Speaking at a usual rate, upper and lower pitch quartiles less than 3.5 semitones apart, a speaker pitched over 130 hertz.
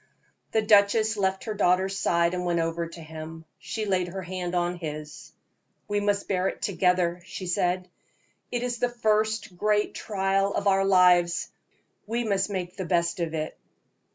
Yes: average, 170 wpm; average, 2.9 semitones; medium, 185 Hz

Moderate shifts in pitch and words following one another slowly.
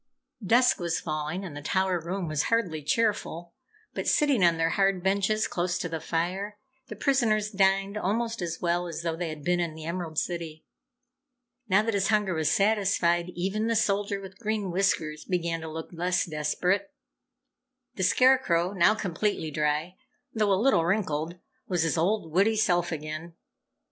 No: average, 3.7 semitones; average, 170 wpm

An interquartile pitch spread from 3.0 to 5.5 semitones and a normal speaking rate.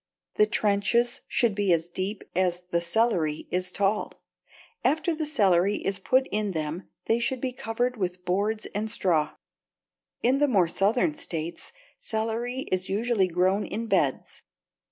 Yes: average, 4.6 semitones; average, 155 wpm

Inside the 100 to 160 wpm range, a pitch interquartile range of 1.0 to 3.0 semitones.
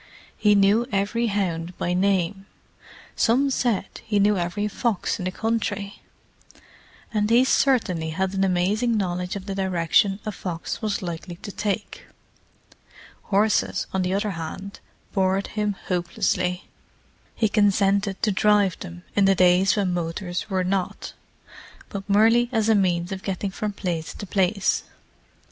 Yes: average, 145 wpm; narrow, 2.5 semitones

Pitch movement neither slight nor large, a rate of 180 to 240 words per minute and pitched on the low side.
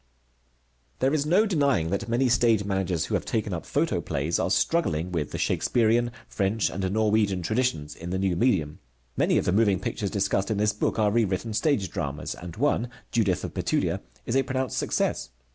Yes: average, 4.7 semitones; average, 185 wpm; low, 105 Hz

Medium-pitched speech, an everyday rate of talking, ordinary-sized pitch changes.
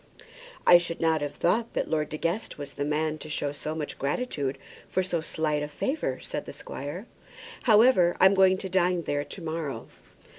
Yes: medium, 160 Hz; average, 190 wpm; average, 4.0 semitones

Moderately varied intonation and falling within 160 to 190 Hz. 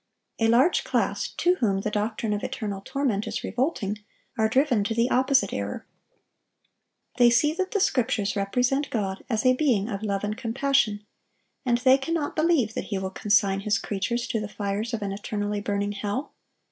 No: average, 4.1 semitones; high, 220 Hz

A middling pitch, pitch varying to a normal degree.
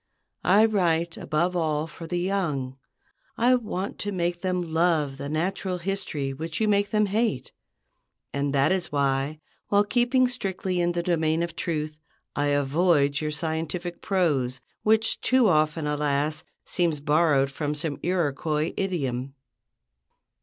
Yes: medium, 165 Hz; average, 4.0 semitones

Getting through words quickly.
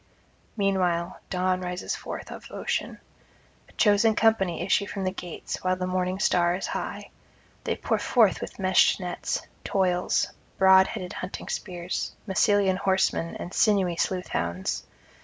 No: average, 140 wpm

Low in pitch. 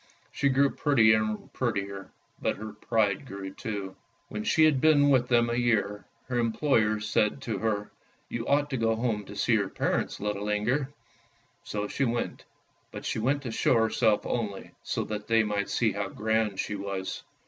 Yes: low, 110 Hz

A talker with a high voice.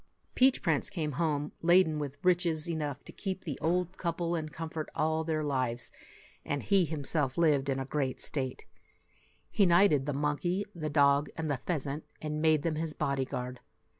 No: medium, 155 Hz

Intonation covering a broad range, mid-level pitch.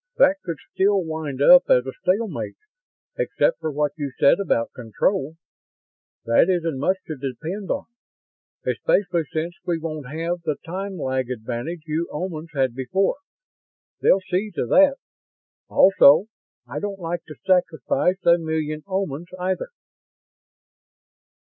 No: average, 4.6 semitones; medium, 165 Hz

